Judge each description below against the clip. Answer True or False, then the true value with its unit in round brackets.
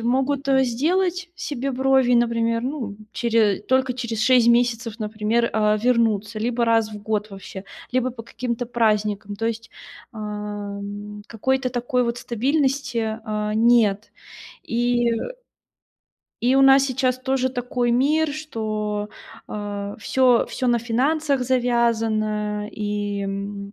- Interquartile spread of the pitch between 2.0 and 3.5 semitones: True (3.1 semitones)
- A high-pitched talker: True (230 Hz)